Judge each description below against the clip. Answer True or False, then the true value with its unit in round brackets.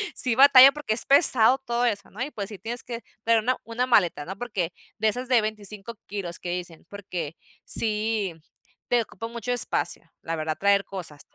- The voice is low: False (215 Hz)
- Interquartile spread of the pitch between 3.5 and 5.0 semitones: True (4.0 semitones)